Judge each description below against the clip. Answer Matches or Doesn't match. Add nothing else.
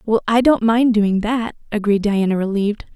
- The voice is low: Doesn't match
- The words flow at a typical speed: Matches